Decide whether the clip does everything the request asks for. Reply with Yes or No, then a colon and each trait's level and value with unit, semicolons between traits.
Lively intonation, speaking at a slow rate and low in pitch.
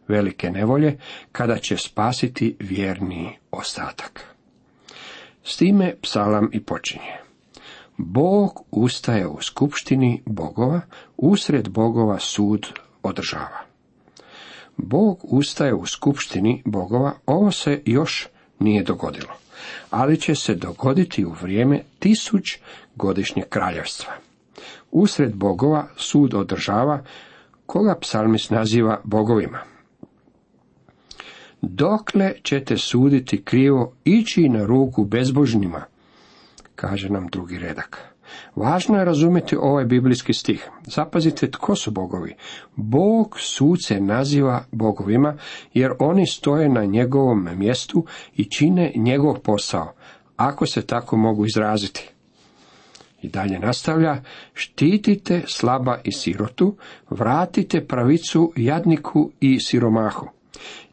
Yes: wide, 6.5 semitones; slow, 100 wpm; low, 125 Hz